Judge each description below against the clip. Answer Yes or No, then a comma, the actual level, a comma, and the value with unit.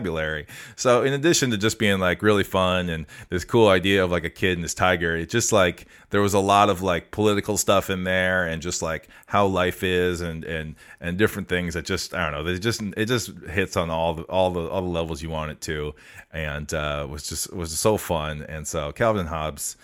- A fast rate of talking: Yes, fast, 235 wpm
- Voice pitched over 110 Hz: No, very low, 90 Hz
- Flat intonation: No, average, 3.7 semitones